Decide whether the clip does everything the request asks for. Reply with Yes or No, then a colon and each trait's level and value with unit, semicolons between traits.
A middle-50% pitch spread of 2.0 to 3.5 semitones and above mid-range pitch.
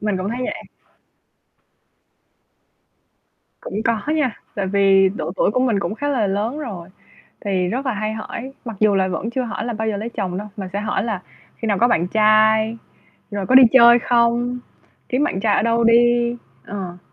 Yes: average, 3.2 semitones; high, 220 Hz